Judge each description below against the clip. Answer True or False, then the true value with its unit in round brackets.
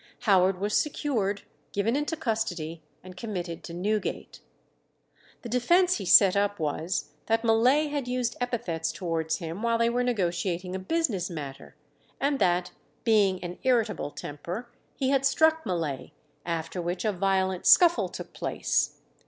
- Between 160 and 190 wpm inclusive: False (145 wpm)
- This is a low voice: False (200 Hz)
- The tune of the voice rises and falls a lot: True (5.7 semitones)